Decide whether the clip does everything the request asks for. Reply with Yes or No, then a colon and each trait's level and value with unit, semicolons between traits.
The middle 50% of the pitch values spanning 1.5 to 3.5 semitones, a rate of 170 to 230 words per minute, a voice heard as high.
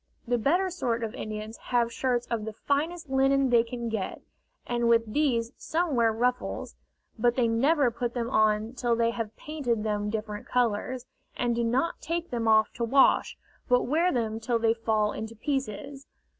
Yes: average, 3.0 semitones; average, 180 wpm; high, 235 Hz